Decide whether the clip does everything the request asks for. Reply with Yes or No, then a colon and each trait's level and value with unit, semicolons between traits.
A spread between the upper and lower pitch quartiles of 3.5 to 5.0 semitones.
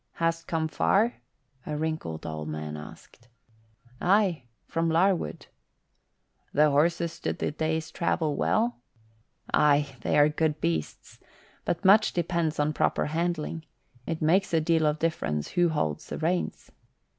No: narrow, 2.5 semitones